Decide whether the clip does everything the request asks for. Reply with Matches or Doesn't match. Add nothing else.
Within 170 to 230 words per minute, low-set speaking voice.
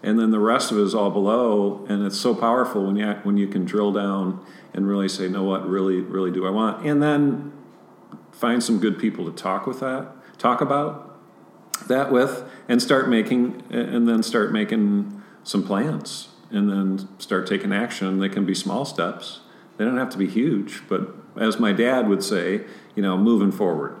Matches